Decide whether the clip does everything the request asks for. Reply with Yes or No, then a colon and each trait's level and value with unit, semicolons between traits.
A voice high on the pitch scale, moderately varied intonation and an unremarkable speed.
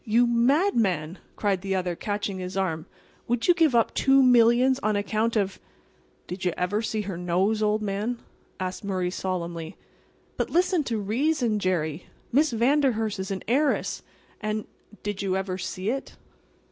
Yes: high, 210 Hz; average, 4.3 semitones; average, 160 wpm